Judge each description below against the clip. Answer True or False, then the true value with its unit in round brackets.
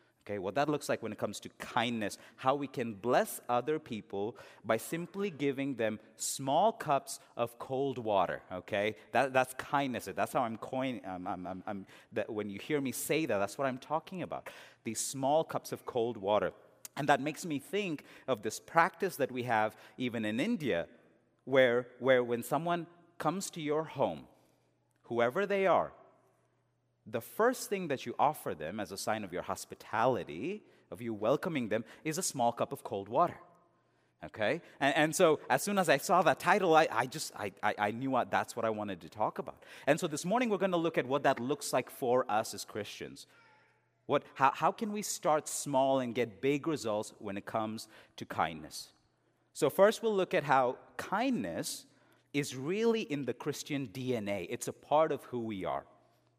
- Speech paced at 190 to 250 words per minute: True (195 wpm)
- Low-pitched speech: True (130 Hz)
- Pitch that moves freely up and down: True (5.7 semitones)